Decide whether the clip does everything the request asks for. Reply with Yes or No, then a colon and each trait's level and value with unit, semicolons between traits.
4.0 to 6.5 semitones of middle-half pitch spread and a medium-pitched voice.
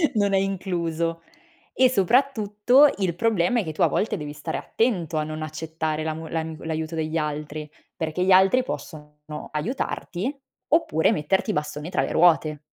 Yes: average, 4.3 semitones; medium, 165 Hz